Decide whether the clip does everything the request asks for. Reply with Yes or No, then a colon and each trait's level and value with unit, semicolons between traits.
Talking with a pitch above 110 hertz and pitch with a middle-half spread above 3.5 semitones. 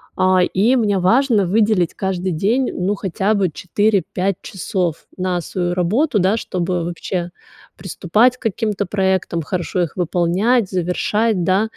No: high, 190 Hz; average, 3.1 semitones